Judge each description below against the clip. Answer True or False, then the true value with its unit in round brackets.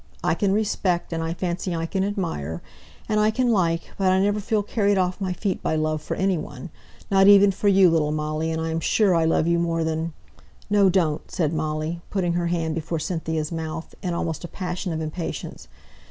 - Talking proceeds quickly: True (210 wpm)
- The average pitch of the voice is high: False (170 Hz)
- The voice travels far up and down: False (3.1 semitones)